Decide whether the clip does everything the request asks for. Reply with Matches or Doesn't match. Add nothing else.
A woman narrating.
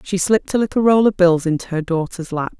Matches